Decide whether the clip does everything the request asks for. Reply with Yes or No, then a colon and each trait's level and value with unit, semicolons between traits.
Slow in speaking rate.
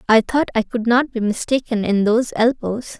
No: average, 200 wpm